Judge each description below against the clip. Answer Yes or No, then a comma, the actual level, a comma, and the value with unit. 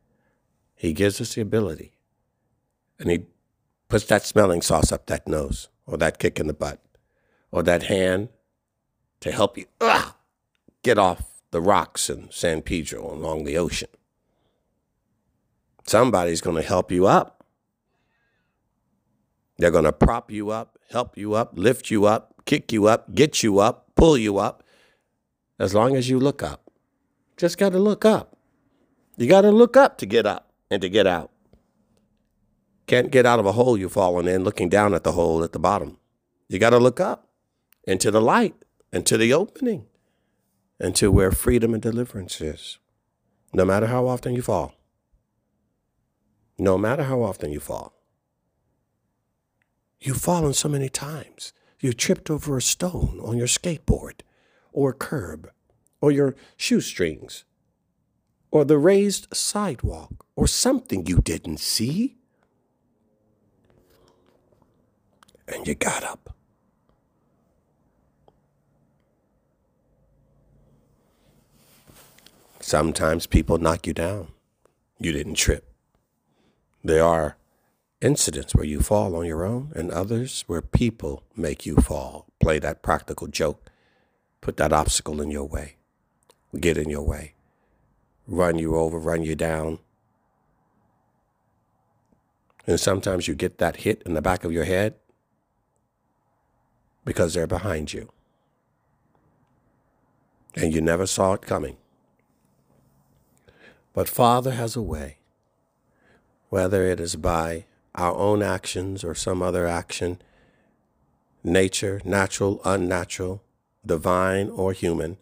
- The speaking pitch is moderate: No, very low, 95 Hz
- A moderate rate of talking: No, slow, 130 wpm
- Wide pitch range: Yes, wide, 6.4 semitones